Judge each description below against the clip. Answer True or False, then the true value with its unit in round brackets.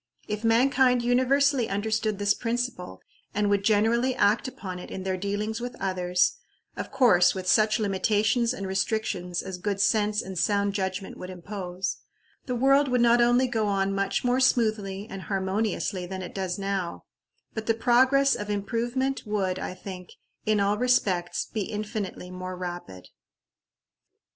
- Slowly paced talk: False (155 wpm)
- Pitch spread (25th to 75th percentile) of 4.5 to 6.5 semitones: False (3.8 semitones)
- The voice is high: True (205 Hz)